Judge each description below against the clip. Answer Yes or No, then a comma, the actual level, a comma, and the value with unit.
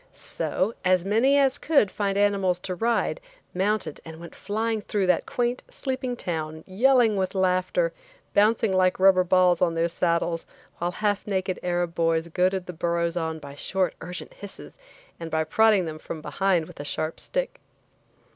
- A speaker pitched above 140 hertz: Yes, medium, 185 Hz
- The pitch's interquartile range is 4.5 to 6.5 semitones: No, average, 3.8 semitones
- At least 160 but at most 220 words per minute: Yes, average, 165 wpm